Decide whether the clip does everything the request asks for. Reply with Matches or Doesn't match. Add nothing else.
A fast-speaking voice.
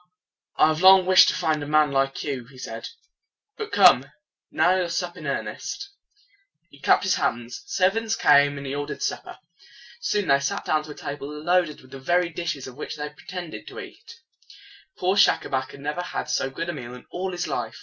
Matches